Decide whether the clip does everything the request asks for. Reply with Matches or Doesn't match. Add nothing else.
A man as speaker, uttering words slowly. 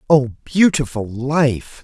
Matches